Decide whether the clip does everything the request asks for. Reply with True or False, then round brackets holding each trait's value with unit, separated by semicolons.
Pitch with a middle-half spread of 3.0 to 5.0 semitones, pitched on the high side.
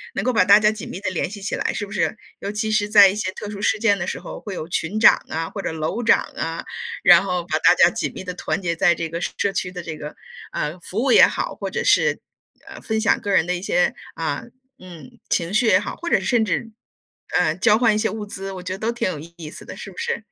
True (3.8 semitones; 195 Hz)